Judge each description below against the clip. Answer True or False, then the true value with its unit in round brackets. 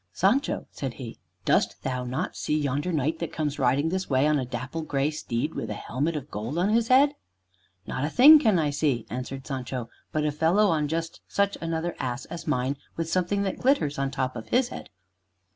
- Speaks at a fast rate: True (210 wpm)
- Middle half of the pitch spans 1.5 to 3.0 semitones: False (4.7 semitones)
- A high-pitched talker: False (150 Hz)